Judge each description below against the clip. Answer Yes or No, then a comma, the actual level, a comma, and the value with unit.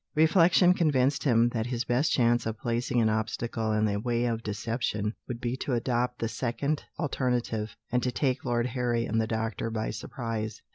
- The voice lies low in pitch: Yes, low, 120 Hz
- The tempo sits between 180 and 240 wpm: Yes, average, 185 wpm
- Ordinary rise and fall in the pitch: No, narrow, 2.1 semitones